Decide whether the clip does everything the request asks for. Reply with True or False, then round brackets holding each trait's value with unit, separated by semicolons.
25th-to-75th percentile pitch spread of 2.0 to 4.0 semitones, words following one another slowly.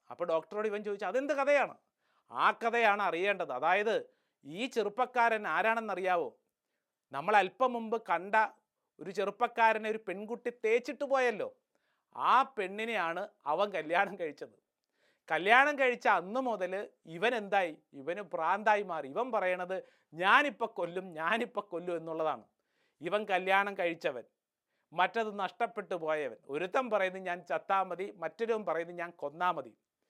False (4.7 semitones; 120 wpm)